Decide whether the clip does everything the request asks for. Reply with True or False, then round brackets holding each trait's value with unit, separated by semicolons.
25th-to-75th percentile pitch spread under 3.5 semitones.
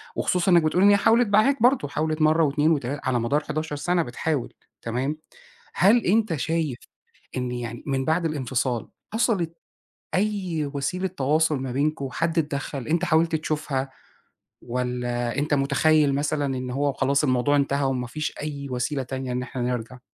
False (3.8 semitones)